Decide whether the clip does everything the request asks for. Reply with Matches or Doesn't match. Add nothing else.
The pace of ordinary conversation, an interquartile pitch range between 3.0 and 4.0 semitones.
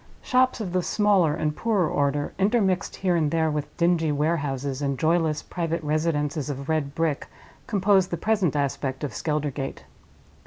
Matches